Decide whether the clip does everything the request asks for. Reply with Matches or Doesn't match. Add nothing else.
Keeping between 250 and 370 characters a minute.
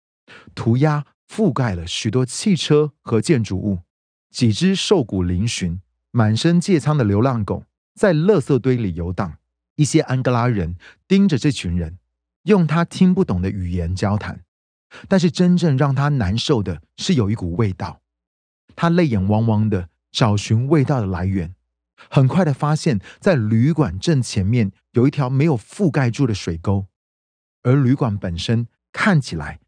Doesn't match